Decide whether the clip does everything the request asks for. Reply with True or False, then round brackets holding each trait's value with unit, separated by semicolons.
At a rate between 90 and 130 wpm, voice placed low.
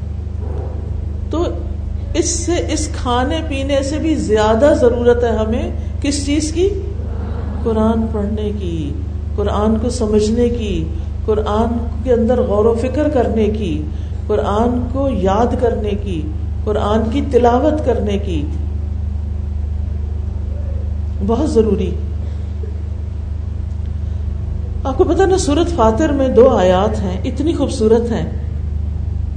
True (110 wpm; 85 Hz)